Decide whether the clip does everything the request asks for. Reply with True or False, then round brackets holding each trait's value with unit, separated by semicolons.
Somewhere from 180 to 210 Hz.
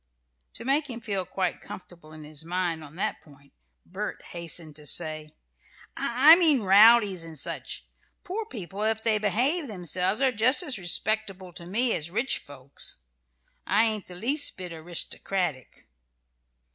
True (190 Hz)